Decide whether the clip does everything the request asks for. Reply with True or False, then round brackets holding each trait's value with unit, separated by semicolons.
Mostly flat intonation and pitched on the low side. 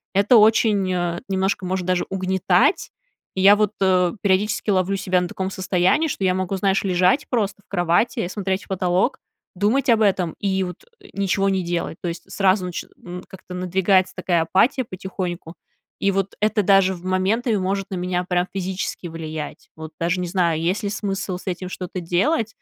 False (1.8 semitones; 190 Hz)